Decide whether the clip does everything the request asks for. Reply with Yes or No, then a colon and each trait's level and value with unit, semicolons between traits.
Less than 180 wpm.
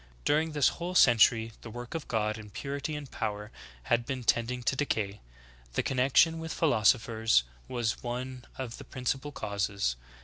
Yes: average, 160 wpm